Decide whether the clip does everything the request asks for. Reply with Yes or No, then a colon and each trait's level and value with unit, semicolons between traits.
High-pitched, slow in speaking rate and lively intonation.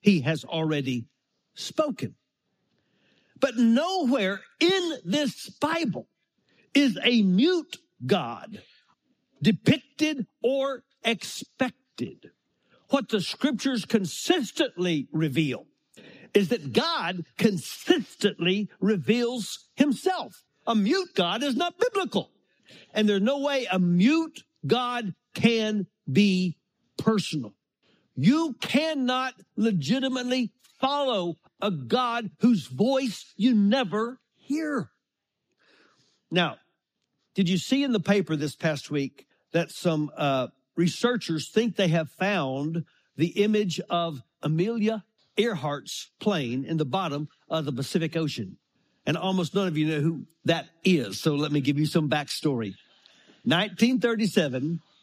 Yes: high, 205 Hz; slow, 110 wpm; wide, 7.3 semitones